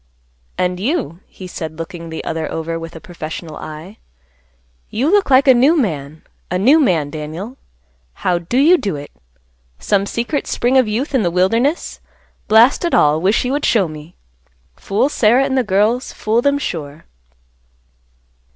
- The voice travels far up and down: Yes, wide, 7.9 semitones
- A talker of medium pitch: No, high, 200 Hz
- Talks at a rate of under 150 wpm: No, average, 165 wpm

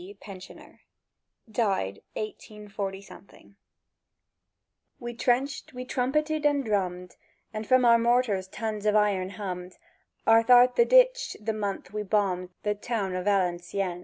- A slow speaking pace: Yes, slow, 120 wpm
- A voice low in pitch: No, high, 210 Hz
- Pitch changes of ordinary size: Yes, average, 4.1 semitones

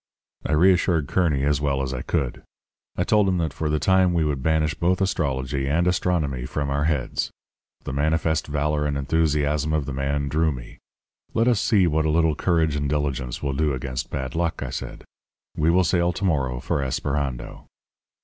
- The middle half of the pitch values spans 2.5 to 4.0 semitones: Yes, average, 3.3 semitones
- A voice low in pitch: Yes, very low, 75 Hz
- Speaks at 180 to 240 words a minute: Yes, average, 190 wpm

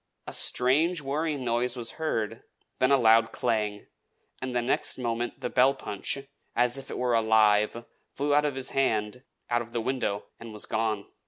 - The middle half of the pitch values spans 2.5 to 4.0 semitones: Yes, average, 3.1 semitones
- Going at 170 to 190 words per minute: Yes, average, 180 wpm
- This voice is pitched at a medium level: No, low, 120 Hz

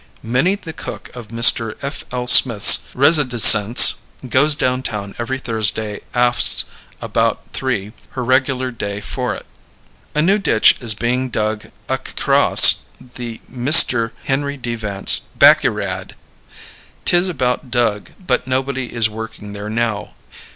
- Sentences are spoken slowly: Yes, slow, 125 wpm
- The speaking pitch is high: No, low, 120 Hz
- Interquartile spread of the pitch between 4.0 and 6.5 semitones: No, average, 3.1 semitones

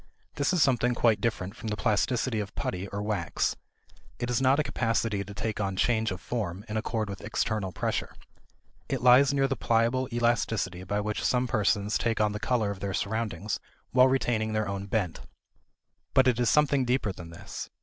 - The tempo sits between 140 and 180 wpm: No, average, 190 wpm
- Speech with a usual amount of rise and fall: Yes, average, 3.3 semitones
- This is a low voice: Yes, low, 110 Hz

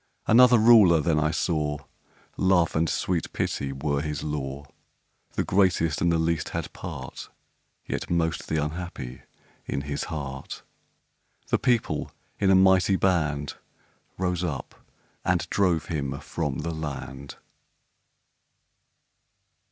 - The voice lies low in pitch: Yes, very low, 80 Hz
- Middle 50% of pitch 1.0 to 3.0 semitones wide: No, average, 3.7 semitones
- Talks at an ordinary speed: No, slow, 120 wpm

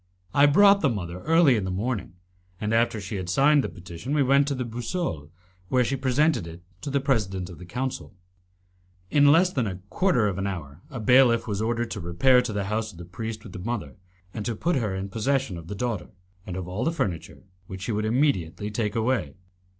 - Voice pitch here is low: Yes, low, 110 Hz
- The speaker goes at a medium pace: No, fast, 220 wpm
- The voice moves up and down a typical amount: No, wide, 5.9 semitones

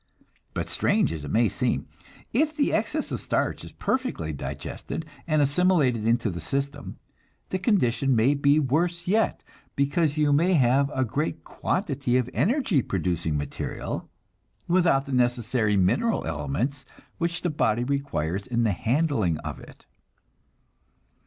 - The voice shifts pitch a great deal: Yes, wide, 6.5 semitones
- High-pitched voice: No, low, 135 Hz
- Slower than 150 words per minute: Yes, average, 140 wpm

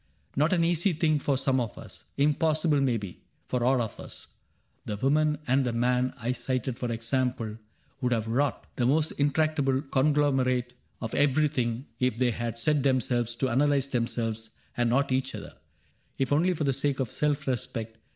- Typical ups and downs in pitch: Yes, average, 3.4 semitones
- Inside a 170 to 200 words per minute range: Yes, average, 175 wpm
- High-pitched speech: No, low, 130 Hz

